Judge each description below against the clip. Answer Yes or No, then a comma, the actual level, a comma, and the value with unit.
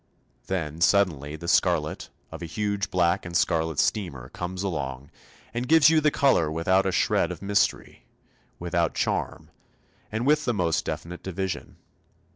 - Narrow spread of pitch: No, average, 3.7 semitones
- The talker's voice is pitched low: Yes, very low, 90 Hz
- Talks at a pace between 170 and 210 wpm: No, average, 150 wpm